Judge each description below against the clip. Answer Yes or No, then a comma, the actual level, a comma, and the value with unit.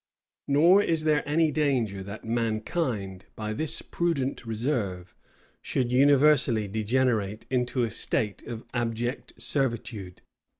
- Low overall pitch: Yes, low, 120 Hz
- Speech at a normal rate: No, slow, 115 wpm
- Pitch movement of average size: Yes, average, 4.7 semitones